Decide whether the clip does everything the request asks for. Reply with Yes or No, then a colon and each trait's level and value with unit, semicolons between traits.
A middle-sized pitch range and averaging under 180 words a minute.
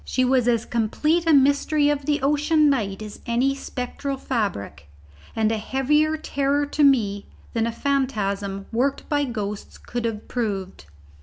Yes: average, 4.9 semitones; average, 155 wpm